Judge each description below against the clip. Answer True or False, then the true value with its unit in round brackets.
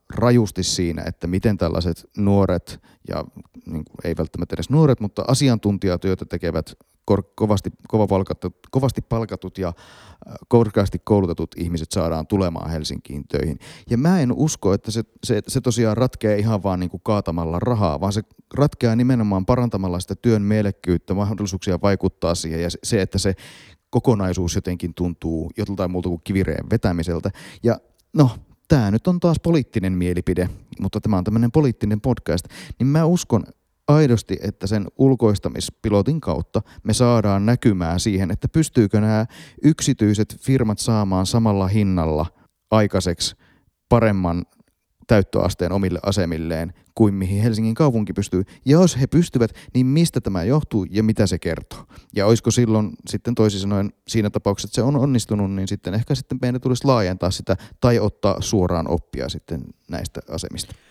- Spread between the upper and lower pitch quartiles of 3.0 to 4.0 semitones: False (4.5 semitones)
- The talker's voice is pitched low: True (100 Hz)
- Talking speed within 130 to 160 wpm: True (150 wpm)